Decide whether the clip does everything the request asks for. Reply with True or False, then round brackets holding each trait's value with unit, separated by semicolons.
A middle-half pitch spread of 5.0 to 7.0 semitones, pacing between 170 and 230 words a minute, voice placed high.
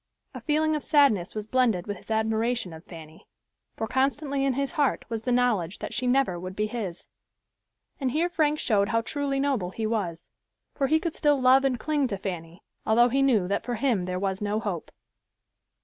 True (5.5 semitones; 200 wpm; 230 Hz)